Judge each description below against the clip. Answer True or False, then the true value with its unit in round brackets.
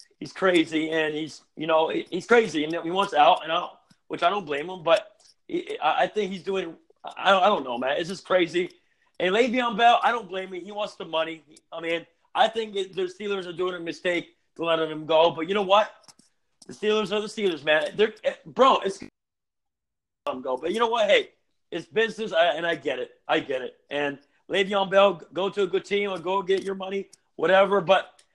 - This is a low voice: False (195 Hz)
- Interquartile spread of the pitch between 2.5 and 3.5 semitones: False (4.7 semitones)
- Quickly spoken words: True (220 wpm)